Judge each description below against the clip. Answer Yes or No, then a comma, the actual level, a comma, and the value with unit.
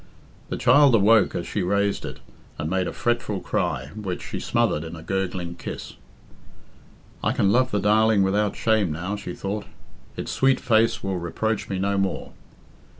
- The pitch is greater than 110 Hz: No, low, 100 Hz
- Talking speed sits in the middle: Yes, average, 170 wpm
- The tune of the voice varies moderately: Yes, average, 3.1 semitones